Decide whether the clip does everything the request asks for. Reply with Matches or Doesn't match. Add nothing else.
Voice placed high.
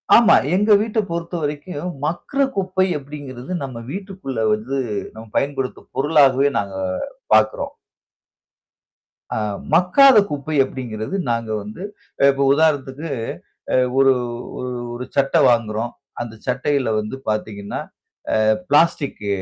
Doesn't match